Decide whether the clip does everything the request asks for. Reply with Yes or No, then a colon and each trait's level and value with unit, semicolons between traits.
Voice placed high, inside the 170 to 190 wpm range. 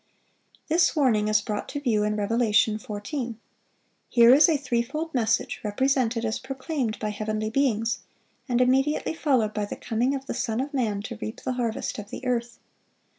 Yes: high, 235 Hz; average, 175 wpm